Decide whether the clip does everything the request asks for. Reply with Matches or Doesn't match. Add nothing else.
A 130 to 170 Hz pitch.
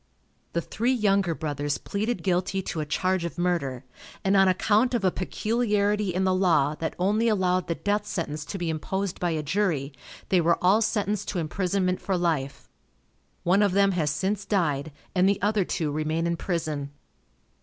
Doesn't match